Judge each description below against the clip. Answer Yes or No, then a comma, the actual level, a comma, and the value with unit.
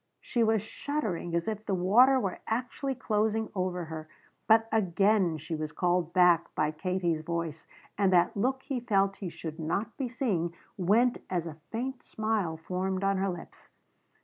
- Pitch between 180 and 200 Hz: Yes, high, 190 Hz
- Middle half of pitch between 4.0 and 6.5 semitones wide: Yes, average, 4.5 semitones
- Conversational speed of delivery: Yes, average, 170 wpm